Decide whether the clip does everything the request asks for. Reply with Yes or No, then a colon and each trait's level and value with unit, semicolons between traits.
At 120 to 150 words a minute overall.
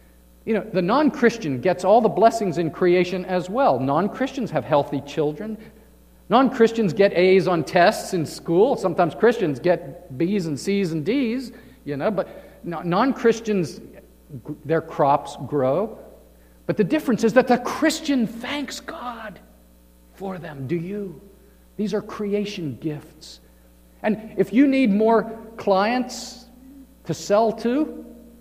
Yes: average, 145 wpm